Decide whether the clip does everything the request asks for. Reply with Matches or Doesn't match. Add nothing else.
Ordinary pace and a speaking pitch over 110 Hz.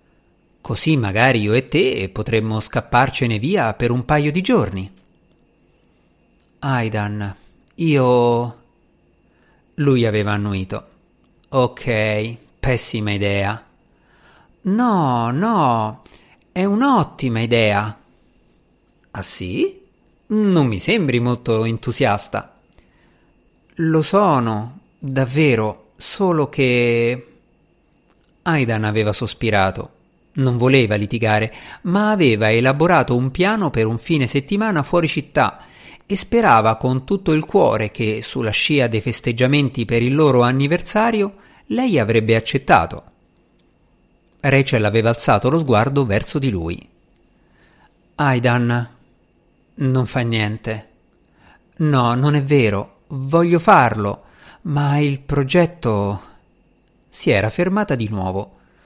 Doesn't match